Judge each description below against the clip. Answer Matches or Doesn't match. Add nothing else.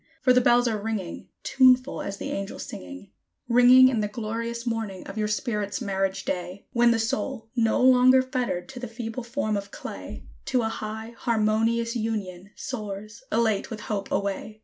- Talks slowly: Doesn't match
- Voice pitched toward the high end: Matches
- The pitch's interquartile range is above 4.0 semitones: Doesn't match